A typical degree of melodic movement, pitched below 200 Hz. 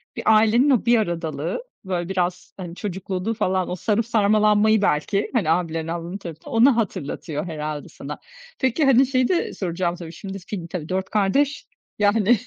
Yes: average, 4.5 semitones; high, 190 Hz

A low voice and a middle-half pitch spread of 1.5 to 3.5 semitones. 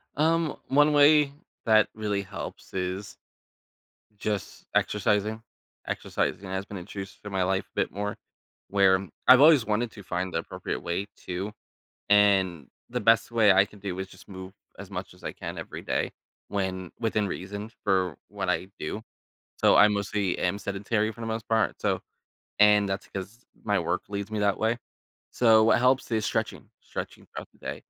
Yes: low, 105 Hz; narrow, 2.6 semitones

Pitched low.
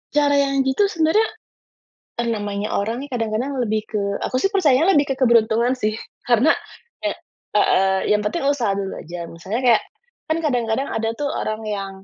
No: high, 235 Hz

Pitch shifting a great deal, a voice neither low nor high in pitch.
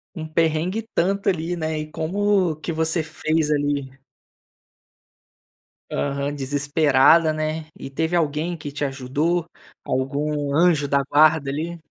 No: narrow, 2.4 semitones; medium, 155 Hz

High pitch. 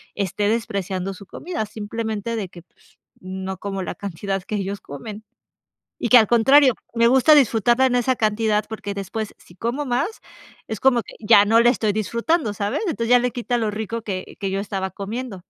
Yes: high, 220 Hz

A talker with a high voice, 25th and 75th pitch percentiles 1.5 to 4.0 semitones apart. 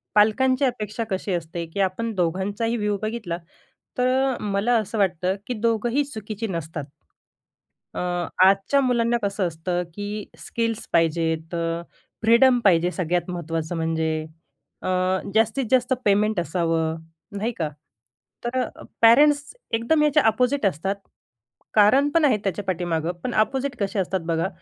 No: high, 205 Hz; average, 5.3 semitones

